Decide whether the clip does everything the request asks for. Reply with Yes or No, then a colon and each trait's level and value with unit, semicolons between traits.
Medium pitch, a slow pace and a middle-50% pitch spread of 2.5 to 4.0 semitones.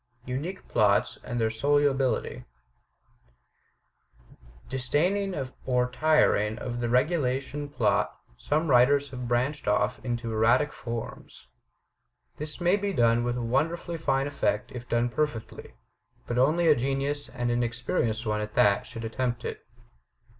No: low, 125 Hz; slow, 130 wpm; average, 3.6 semitones